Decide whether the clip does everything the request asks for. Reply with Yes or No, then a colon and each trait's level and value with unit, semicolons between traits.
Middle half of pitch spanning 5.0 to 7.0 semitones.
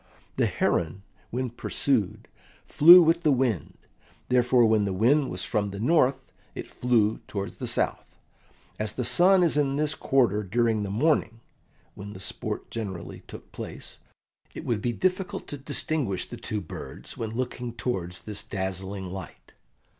Yes: average, 5.3 semitones